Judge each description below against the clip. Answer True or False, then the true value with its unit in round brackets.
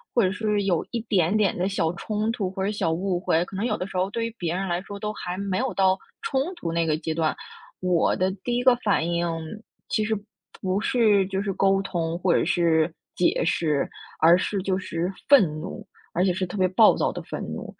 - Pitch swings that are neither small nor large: True (3.2 semitones)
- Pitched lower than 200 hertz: True (190 Hz)